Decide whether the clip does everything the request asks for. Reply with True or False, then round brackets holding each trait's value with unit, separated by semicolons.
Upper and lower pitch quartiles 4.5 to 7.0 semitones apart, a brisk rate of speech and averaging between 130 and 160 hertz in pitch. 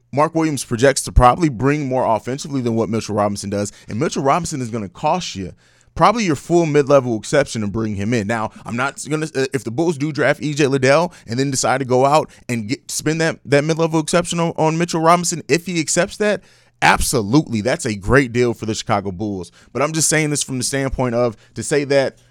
True (5.0 semitones; 225 wpm; 135 Hz)